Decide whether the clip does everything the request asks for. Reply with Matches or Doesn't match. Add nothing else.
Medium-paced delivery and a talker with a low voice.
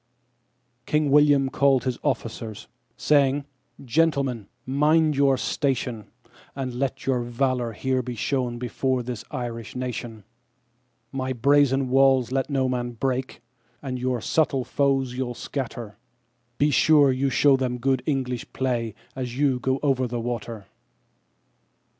Doesn't match